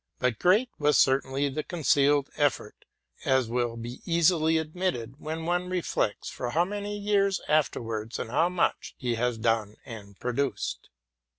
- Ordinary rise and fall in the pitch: No, wide, 6.2 semitones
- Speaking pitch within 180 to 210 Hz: No, medium, 145 Hz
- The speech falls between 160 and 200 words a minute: No, average, 150 wpm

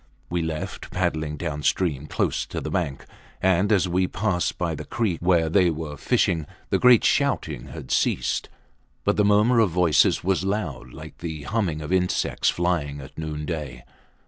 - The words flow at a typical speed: Yes, average, 165 wpm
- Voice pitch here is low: Yes, very low, 85 Hz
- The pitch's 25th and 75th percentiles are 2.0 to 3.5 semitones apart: No, average, 3.9 semitones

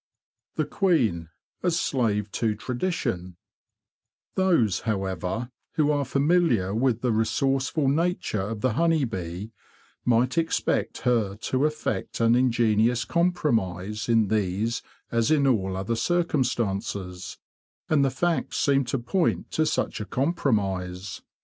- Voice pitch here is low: Yes, low, 115 Hz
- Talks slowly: Yes, slow, 125 wpm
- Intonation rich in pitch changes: Yes, wide, 6.0 semitones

